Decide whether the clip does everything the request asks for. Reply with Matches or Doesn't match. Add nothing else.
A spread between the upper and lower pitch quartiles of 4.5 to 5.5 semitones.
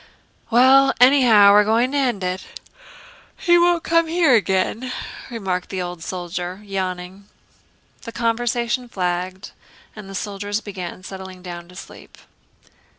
Matches